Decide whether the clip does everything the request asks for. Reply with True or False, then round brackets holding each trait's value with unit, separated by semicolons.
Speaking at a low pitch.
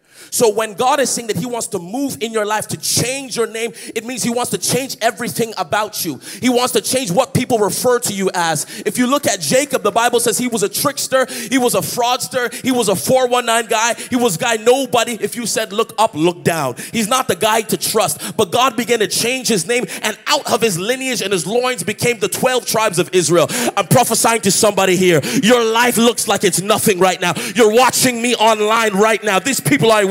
False (230 Hz)